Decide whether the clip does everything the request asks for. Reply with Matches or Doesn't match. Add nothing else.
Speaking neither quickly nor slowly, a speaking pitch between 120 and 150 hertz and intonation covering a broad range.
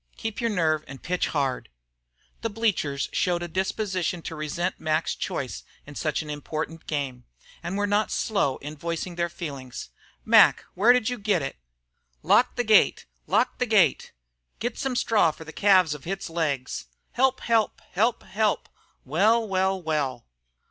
Doesn't match